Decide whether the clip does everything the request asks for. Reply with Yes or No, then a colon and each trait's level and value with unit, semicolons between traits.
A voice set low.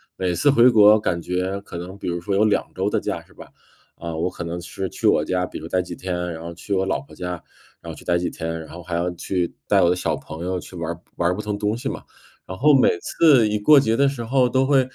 Yes: very low, 95 Hz